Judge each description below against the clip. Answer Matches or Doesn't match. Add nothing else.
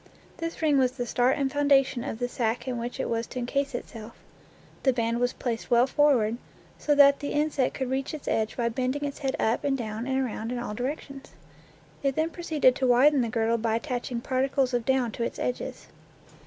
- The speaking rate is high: Matches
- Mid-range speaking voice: Doesn't match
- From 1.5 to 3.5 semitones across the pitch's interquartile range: Matches